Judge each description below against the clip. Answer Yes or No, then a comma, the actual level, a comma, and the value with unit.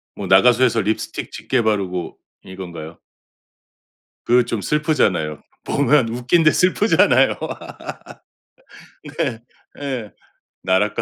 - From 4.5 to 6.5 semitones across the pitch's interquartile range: Yes, wide, 5.6 semitones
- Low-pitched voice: Yes, low, 115 Hz